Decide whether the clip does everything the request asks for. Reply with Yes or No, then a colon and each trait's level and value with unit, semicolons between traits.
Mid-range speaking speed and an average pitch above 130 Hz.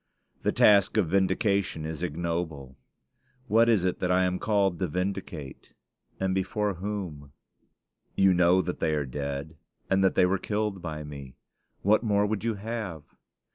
No: average, 160 wpm; very low, 90 Hz